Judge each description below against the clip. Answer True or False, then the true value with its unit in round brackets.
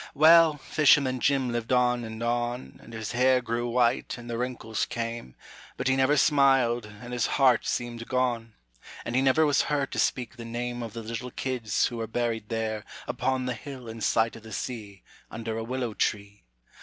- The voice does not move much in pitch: True (2.2 semitones)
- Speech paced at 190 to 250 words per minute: True (195 wpm)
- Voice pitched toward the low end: True (120 Hz)